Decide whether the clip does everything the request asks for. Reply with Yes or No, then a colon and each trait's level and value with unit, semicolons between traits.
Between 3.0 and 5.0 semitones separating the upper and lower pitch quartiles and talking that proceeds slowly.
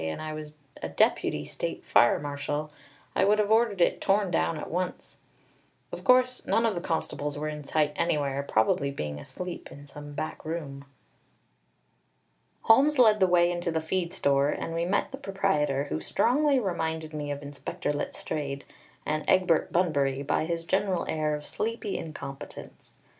No: average, 4.7 semitones; average, 165 wpm